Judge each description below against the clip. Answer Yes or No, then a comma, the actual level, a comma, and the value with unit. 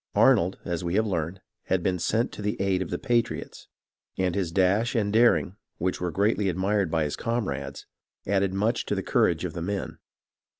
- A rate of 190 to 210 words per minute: Yes, average, 195 wpm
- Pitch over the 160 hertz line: No, very low, 95 Hz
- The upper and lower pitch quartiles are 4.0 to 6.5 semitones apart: No, average, 2.8 semitones